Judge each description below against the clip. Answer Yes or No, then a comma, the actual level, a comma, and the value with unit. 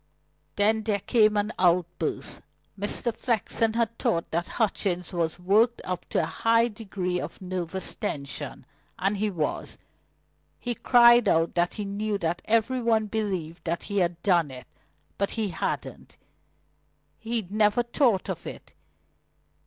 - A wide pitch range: No, average, 4.0 semitones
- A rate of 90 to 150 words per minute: Yes, average, 145 wpm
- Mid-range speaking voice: No, high, 205 Hz